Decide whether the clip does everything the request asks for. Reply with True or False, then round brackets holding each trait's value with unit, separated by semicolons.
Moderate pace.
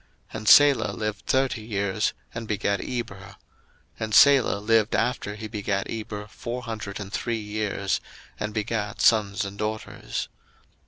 True (150 wpm)